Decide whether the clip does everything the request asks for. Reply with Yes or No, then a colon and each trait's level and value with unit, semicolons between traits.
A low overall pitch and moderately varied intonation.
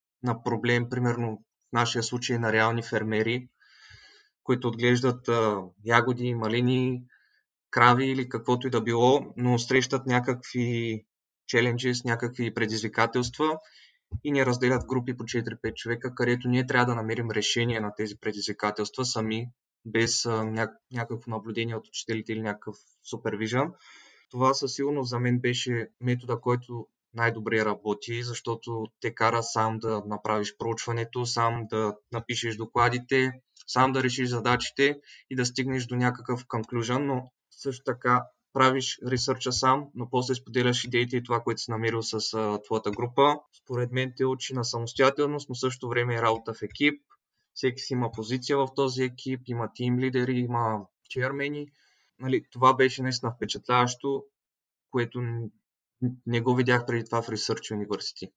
No: low, 120 Hz; narrow, 2.1 semitones